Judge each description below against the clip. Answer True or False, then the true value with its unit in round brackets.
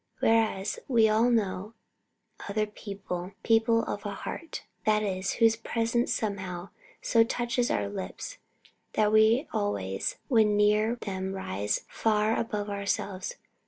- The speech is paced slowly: True (125 wpm)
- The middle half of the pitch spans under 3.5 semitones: True (2.7 semitones)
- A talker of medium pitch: False (210 Hz)